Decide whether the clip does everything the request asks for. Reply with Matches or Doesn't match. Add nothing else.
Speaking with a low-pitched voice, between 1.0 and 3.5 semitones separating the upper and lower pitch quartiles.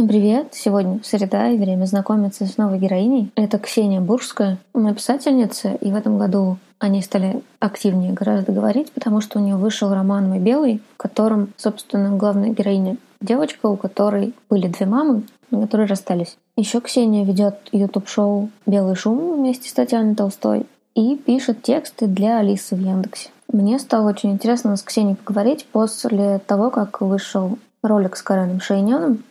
Doesn't match